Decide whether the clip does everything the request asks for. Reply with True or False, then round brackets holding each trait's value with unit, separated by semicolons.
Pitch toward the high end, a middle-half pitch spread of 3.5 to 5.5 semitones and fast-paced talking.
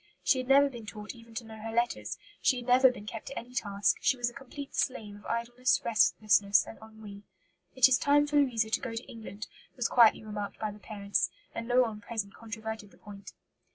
False (225 Hz; 2.9 semitones; 220 wpm)